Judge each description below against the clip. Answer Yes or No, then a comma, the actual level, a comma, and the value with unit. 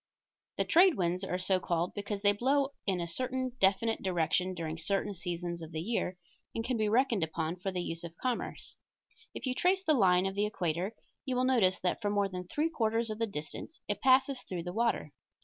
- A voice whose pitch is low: No, high, 200 Hz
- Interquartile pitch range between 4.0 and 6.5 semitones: Yes, average, 5.3 semitones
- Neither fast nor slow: No, fast, 215 wpm